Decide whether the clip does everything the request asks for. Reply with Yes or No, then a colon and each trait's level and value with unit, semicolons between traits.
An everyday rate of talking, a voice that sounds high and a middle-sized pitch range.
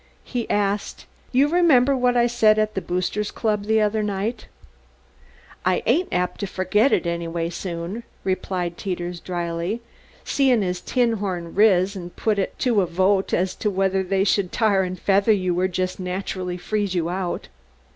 Yes: average, 165 wpm; high, 195 Hz; average, 3.1 semitones